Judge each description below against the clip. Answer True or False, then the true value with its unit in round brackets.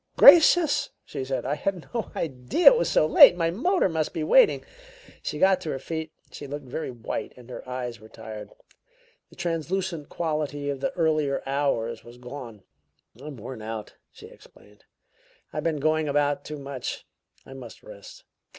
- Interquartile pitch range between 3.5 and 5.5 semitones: True (4.5 semitones)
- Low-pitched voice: False (145 Hz)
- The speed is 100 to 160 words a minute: False (170 wpm)